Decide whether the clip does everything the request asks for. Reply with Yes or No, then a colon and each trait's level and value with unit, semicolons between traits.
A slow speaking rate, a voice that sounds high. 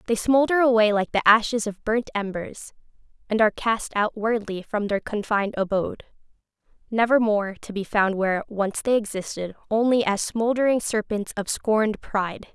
No: average, 160 wpm; high, 215 Hz